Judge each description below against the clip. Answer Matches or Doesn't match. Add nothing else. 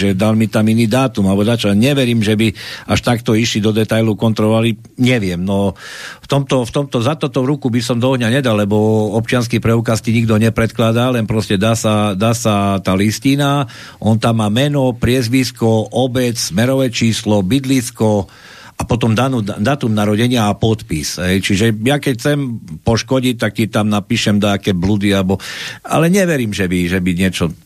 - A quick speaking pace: Matches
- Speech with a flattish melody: Doesn't match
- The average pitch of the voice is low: Matches